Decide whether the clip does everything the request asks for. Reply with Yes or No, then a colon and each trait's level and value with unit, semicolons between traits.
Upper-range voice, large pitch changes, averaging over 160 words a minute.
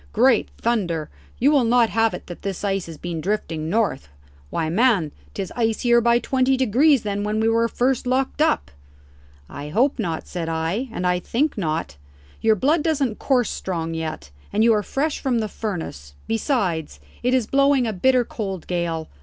Yes: high, 220 Hz; wide, 6.5 semitones; average, 180 wpm